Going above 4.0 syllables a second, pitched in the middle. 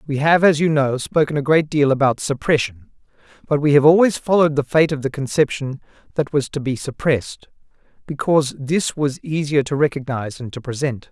Yes: 5.6 syllables/s; medium, 145 Hz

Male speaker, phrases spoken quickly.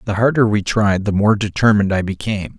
Yes: male; fast, 210 wpm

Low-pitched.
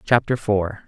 Yes: low, 105 Hz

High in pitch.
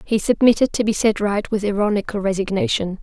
Yes: high, 205 Hz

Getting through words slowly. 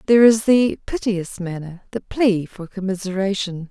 Yes: slow, 130 wpm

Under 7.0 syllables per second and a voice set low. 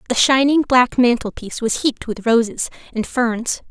No: 5.1 syllables/s; high, 240 Hz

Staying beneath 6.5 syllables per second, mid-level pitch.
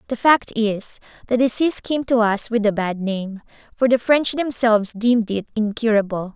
No: 5.0 syllables/s; high, 225 Hz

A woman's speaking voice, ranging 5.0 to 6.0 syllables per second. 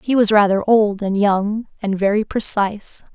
No: female; 4.6 syllables/s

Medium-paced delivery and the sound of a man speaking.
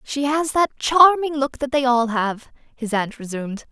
No: average, 195 wpm; female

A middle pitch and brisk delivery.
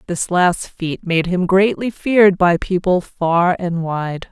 No: medium, 180 Hz; average, 165 wpm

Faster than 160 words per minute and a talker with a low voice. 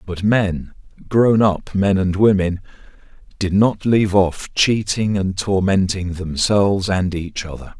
No: average, 140 wpm; very low, 95 Hz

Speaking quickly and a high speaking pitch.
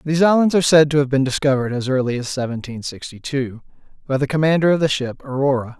No: fast, 220 wpm; medium, 140 Hz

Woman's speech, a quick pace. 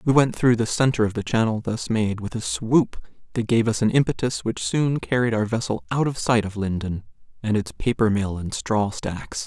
No: male; fast, 220 wpm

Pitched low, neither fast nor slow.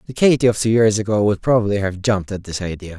No: low, 105 Hz; fast, 260 wpm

